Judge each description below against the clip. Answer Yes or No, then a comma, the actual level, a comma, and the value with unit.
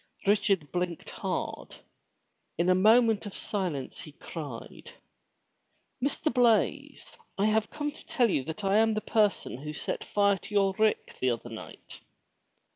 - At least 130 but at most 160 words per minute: Yes, average, 150 wpm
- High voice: Yes, high, 200 Hz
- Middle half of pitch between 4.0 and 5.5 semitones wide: Yes, average, 4.9 semitones